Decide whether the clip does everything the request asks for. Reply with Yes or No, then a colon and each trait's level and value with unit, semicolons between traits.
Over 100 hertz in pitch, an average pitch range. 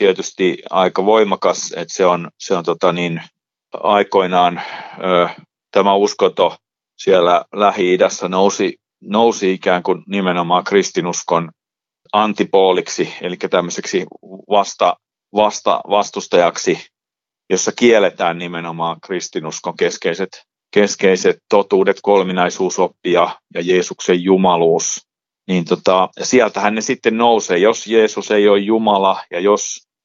No: very low, 95 Hz; average, 3.0 semitones